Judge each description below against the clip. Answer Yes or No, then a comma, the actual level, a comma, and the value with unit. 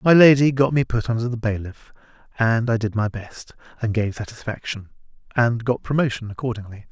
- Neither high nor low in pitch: No, low, 115 Hz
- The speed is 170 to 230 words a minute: Yes, average, 175 wpm